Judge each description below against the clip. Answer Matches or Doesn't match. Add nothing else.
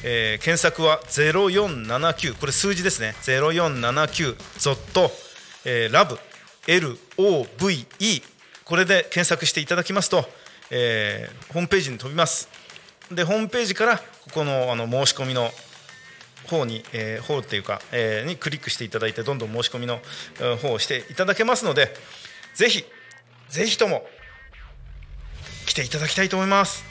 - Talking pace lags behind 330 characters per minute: Matches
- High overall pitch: Doesn't match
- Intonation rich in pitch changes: Matches